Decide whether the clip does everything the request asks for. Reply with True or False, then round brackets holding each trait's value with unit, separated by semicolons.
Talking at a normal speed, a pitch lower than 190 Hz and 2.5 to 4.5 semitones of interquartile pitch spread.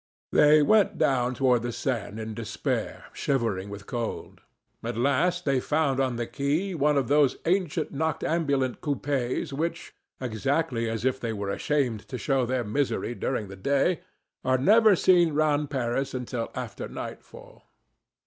True (150 wpm; 135 Hz; 4.0 semitones)